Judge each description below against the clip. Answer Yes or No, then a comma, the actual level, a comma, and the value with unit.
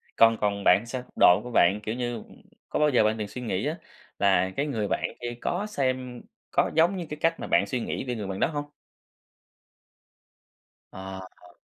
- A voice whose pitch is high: No, low, 120 Hz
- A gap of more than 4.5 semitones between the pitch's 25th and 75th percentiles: Yes, average, 5.1 semitones